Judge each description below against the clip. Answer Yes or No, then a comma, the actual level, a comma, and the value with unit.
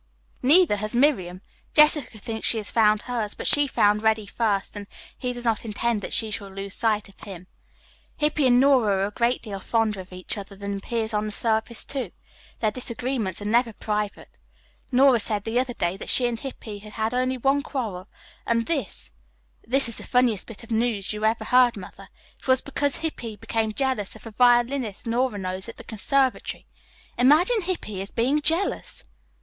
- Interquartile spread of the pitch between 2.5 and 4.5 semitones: Yes, average, 3.6 semitones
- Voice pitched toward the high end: Yes, high, 225 Hz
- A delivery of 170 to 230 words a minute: Yes, average, 190 wpm